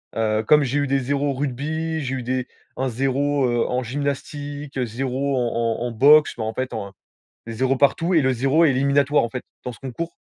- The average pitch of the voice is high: No, low, 135 Hz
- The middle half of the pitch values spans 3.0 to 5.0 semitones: No, narrow, 2.6 semitones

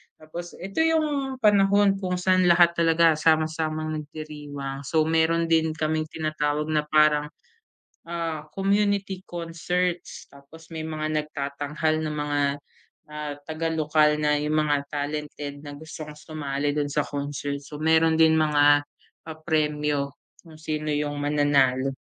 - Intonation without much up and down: Yes, narrow, 1.8 semitones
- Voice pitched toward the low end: No, medium, 155 Hz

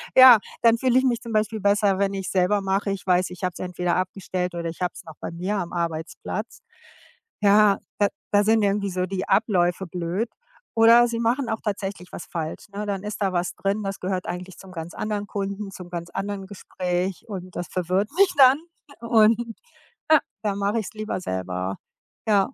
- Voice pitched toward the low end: No, high, 195 Hz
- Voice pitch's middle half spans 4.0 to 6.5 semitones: No, average, 2.9 semitones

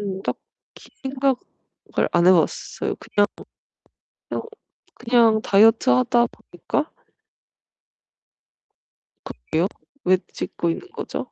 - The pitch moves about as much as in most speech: Yes, average, 5.0 semitones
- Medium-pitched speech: No, high, 205 Hz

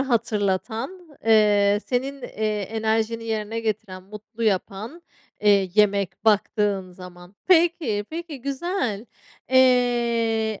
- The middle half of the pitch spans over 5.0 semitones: No, average, 3.3 semitones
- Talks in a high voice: Yes, high, 220 Hz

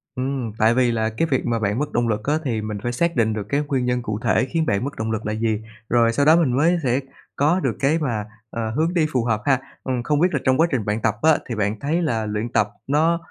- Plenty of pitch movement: No, average, 4.8 semitones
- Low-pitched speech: Yes, low, 125 Hz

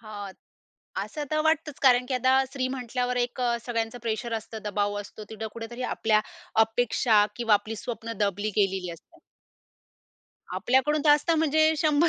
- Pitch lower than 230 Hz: No, high, 240 Hz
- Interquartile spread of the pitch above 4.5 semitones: No, average, 3.7 semitones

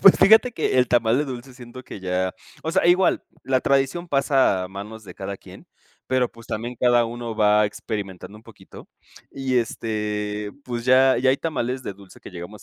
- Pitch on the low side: Yes, low, 120 Hz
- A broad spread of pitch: No, average, 4.0 semitones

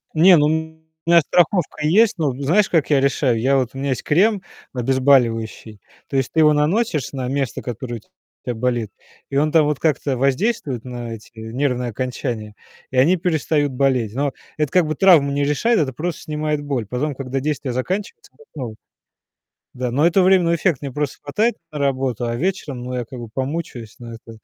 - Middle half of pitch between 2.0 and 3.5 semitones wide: No, average, 4.0 semitones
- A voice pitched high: No, medium, 140 Hz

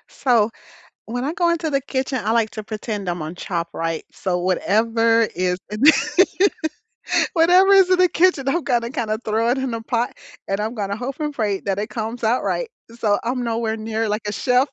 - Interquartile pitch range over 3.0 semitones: Yes, average, 4.4 semitones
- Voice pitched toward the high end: Yes, high, 230 Hz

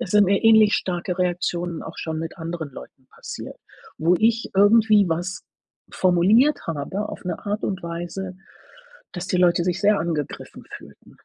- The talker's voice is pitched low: No, medium, 180 Hz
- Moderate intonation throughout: Yes, average, 3.1 semitones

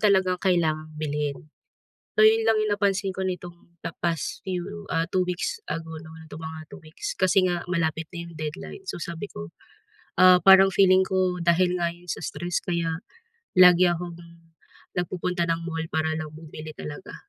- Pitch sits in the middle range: Yes, medium, 175 Hz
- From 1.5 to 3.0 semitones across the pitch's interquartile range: Yes, narrow, 2.5 semitones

